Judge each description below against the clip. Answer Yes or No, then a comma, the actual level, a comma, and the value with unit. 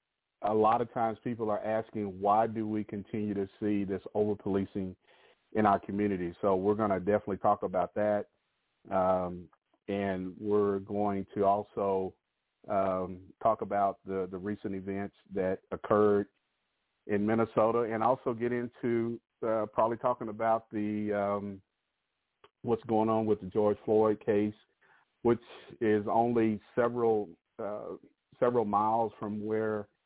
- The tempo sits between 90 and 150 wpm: Yes, average, 140 wpm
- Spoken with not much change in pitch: Yes, narrow, 2.0 semitones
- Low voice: Yes, low, 105 Hz